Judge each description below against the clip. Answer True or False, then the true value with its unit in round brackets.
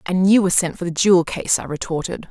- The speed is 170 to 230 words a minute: False (260 wpm)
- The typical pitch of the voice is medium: True (180 Hz)